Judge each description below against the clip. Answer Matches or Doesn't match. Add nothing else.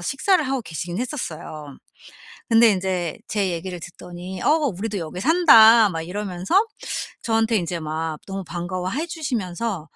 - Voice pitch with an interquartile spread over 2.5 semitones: Matches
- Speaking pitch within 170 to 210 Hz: Matches